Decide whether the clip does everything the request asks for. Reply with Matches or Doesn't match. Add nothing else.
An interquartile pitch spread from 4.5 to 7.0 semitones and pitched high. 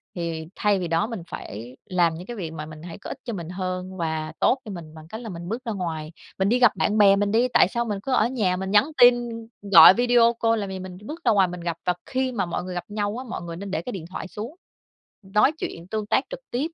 Matches